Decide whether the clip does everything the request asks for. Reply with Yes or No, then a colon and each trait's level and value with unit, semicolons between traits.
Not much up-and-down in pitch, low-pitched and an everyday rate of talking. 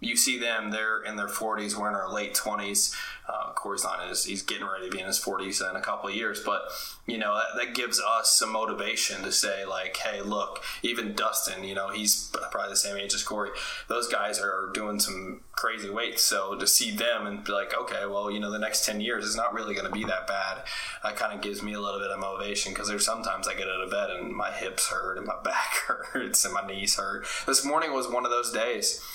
No: narrow, 1.6 semitones; low, 105 Hz; fast, 250 wpm